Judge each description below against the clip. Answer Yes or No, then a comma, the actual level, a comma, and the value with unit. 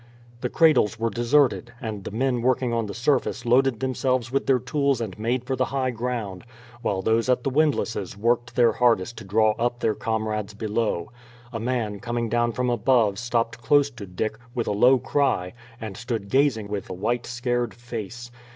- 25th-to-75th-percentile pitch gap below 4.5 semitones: Yes, narrow, 2.5 semitones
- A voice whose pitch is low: Yes, low, 120 Hz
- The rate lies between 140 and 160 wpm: No, average, 190 wpm